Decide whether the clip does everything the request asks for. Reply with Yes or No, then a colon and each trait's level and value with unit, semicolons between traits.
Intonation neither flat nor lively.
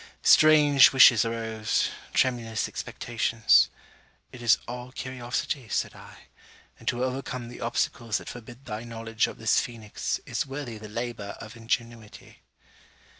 No: narrow, 1.9 semitones